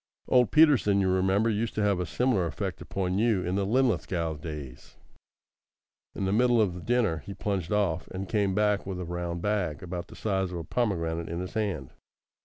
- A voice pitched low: Yes, very low, 95 Hz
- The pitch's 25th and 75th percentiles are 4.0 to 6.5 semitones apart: No, average, 3.5 semitones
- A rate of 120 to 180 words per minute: No, average, 195 wpm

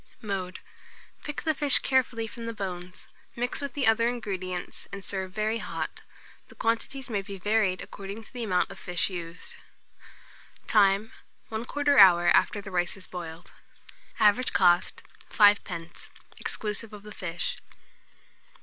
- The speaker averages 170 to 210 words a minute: No, average, 140 wpm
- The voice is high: Yes, high, 205 Hz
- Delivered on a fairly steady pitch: No, average, 3.8 semitones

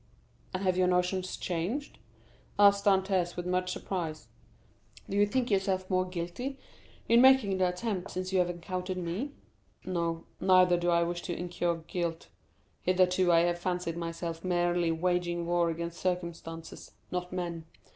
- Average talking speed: Yes, average, 150 wpm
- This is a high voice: No, medium, 180 Hz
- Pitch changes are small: Yes, narrow, 1.5 semitones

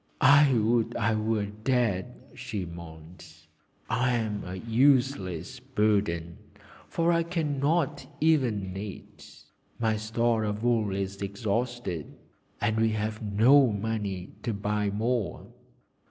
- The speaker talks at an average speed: No, slow, 115 wpm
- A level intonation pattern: No, average, 3.8 semitones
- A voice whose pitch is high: No, low, 110 Hz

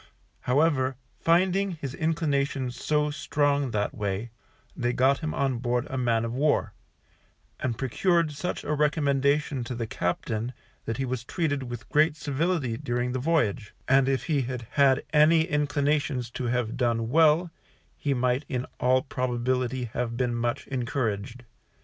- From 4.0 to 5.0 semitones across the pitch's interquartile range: No, average, 3.5 semitones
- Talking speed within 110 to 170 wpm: Yes, average, 150 wpm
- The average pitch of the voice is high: No, low, 130 Hz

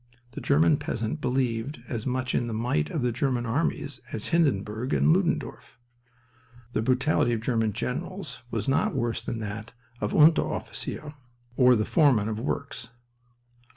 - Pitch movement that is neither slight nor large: Yes, average, 4.1 semitones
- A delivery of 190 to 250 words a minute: No, average, 155 wpm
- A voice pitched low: Yes, low, 125 Hz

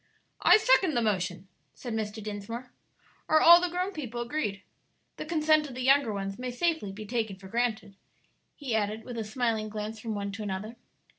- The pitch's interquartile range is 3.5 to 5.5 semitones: Yes, average, 4.9 semitones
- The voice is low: No, high, 225 Hz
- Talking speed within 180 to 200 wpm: Yes, average, 190 wpm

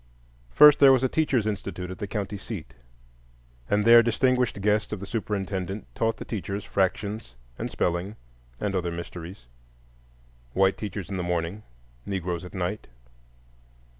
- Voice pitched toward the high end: No, very low, 95 Hz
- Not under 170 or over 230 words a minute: No, average, 140 wpm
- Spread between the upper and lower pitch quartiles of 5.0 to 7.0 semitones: No, average, 3.7 semitones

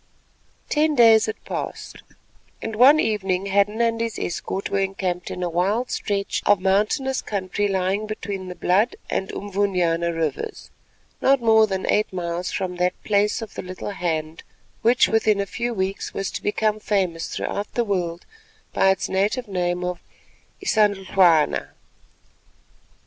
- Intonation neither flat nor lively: Yes, average, 3.1 semitones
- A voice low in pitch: No, high, 195 Hz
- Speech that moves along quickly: No, average, 150 wpm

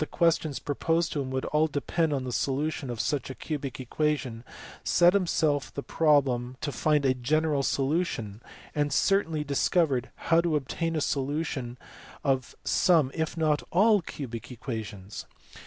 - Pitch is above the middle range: No, medium, 145 Hz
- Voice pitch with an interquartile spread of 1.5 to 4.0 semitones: Yes, average, 3.5 semitones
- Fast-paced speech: No, average, 145 wpm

